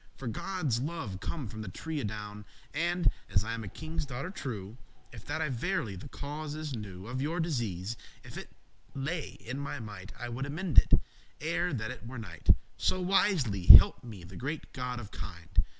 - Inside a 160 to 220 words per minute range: Yes, average, 195 wpm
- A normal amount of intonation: No, wide, 6.8 semitones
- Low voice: Yes, low, 125 Hz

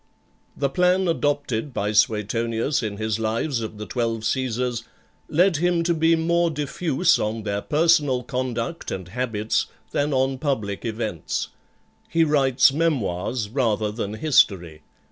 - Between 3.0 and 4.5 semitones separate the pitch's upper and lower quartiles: No, wide, 5.6 semitones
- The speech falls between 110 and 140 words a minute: Yes, slow, 135 wpm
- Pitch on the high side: No, low, 125 Hz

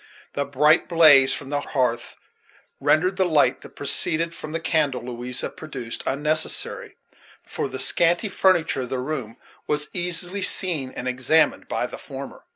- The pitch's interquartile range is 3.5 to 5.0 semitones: Yes, average, 4.2 semitones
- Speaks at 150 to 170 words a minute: Yes, average, 155 wpm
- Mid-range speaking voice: Yes, medium, 150 Hz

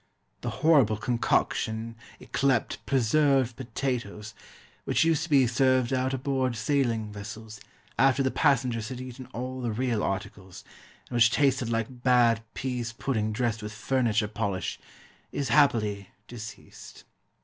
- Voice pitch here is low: Yes, low, 120 Hz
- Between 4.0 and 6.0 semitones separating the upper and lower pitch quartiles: No, average, 3.1 semitones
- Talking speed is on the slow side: Yes, slow, 130 wpm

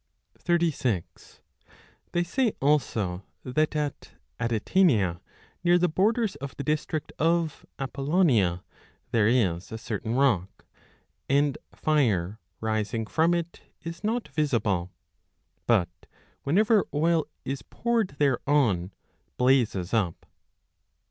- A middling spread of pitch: No, wide, 7.4 semitones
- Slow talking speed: Yes, slow, 100 wpm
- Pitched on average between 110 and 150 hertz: Yes, low, 135 Hz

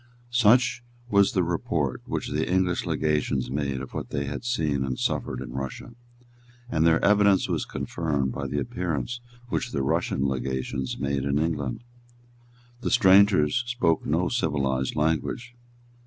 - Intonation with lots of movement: Yes, wide, 5.8 semitones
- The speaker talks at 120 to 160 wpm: Yes, average, 145 wpm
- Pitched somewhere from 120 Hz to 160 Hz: No, very low, 75 Hz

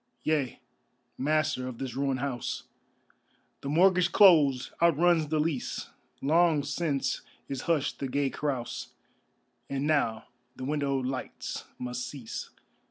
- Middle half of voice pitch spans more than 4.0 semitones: No, average, 3.2 semitones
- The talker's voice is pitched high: No, medium, 140 Hz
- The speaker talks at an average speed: No, slow, 120 wpm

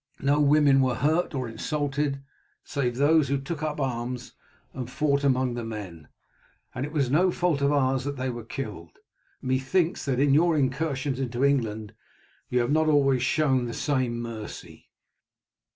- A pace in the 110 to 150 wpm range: No, average, 165 wpm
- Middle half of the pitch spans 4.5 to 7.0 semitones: No, average, 2.9 semitones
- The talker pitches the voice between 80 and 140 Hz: Yes, low, 135 Hz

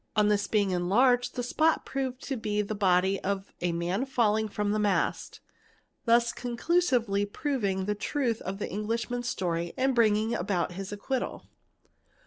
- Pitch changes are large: No, average, 3.8 semitones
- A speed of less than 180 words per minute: Yes, average, 160 wpm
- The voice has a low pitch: No, high, 215 Hz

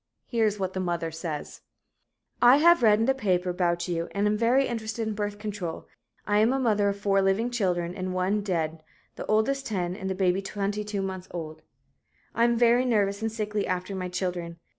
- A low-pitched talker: No, high, 200 Hz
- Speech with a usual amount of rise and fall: Yes, average, 3.4 semitones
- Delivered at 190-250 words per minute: Yes, average, 200 wpm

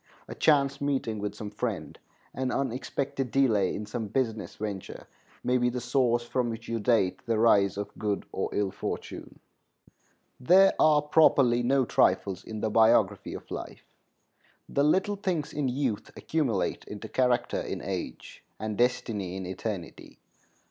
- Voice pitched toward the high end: No, low, 120 Hz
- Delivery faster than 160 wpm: No, average, 150 wpm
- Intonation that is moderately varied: Yes, average, 4.4 semitones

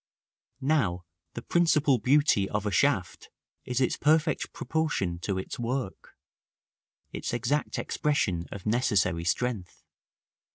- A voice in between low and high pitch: No, low, 120 Hz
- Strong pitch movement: Yes, wide, 7.3 semitones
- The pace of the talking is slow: Yes, slow, 115 wpm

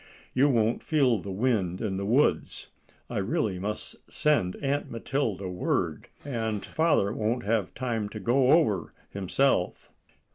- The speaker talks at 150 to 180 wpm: No, average, 140 wpm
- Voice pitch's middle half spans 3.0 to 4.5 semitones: No, average, 5.3 semitones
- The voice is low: Yes, low, 110 Hz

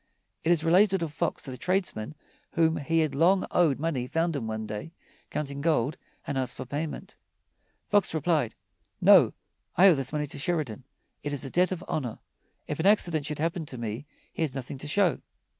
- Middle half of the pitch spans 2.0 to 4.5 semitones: Yes, average, 3.8 semitones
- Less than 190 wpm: No, average, 195 wpm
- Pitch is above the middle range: No, medium, 150 Hz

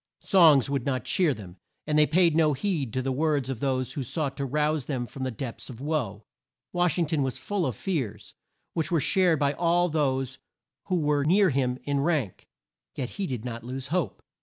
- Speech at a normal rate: No, fast, 210 wpm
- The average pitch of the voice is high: No, medium, 140 Hz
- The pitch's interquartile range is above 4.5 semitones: No, average, 3.8 semitones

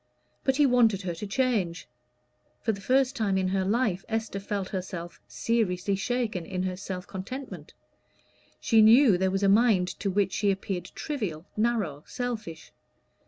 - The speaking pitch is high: Yes, high, 200 Hz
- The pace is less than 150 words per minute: No, average, 160 wpm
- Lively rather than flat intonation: No, average, 3.9 semitones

